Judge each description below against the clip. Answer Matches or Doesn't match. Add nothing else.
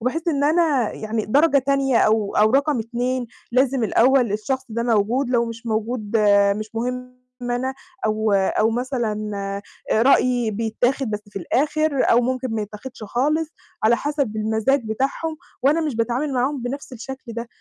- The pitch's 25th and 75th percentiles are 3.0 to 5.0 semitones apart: Matches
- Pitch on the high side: Matches